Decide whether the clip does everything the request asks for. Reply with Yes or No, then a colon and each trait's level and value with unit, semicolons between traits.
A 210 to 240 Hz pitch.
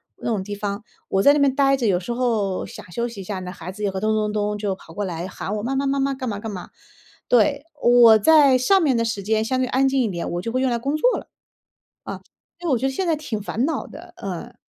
Yes: high, 230 Hz